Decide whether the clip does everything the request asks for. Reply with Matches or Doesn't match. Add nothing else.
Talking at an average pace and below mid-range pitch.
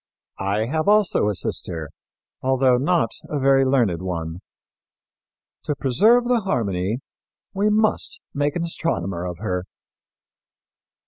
Doesn't match